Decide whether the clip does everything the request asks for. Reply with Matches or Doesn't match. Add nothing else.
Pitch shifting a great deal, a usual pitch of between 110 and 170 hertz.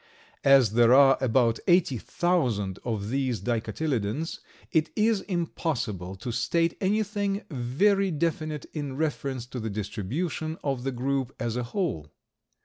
Matches